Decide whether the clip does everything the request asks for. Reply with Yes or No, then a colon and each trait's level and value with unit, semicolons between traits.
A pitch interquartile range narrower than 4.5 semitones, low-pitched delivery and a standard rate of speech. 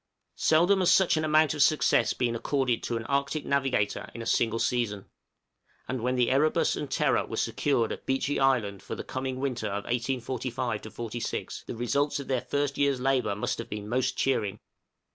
Yes: average, 3.3 semitones; low, 130 Hz; average, 185 wpm